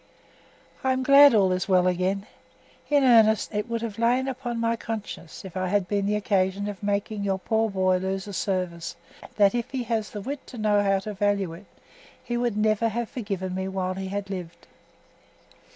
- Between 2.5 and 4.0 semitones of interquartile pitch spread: Yes, average, 3.3 semitones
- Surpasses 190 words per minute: Yes, average, 200 wpm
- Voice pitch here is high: Yes, high, 205 Hz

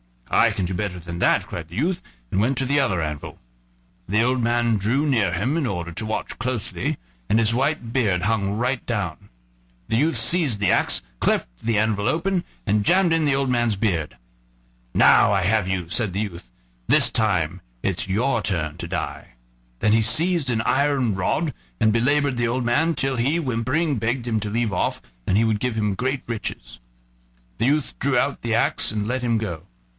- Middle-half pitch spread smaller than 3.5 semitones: No, average, 4.8 semitones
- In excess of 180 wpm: Yes, average, 200 wpm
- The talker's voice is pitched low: Yes, low, 115 Hz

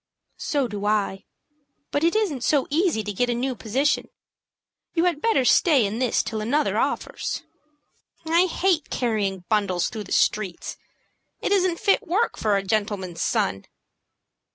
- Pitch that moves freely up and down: Yes, wide, 7.7 semitones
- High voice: Yes, high, 245 Hz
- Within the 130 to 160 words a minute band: Yes, average, 155 wpm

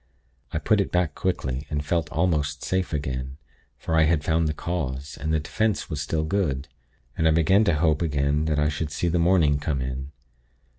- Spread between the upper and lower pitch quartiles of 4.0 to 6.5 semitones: No, average, 3.0 semitones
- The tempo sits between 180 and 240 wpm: Yes, average, 200 wpm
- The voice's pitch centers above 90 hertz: No, very low, 75 Hz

